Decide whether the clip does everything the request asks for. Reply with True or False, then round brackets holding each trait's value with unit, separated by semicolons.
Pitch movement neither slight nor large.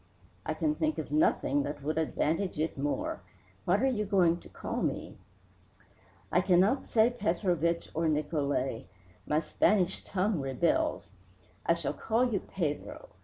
False (5.8 semitones)